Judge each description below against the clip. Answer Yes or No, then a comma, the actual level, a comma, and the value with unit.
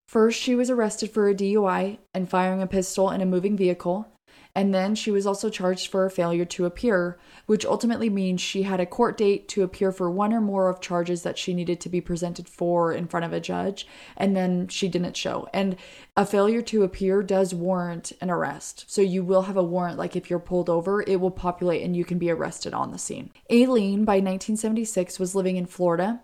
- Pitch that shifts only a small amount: Yes, narrow, 2.2 semitones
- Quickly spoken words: Yes, fast, 220 wpm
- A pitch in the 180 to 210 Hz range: Yes, high, 190 Hz